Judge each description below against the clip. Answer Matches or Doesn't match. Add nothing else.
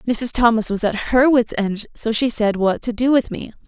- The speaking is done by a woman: Matches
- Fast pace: Matches